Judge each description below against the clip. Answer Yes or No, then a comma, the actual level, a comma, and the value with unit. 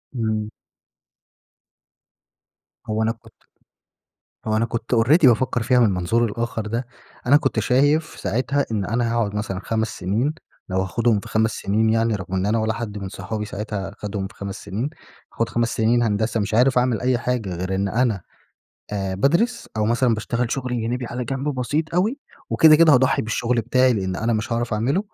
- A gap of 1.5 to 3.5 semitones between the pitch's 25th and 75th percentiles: Yes, average, 3.0 semitones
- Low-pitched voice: Yes, low, 115 Hz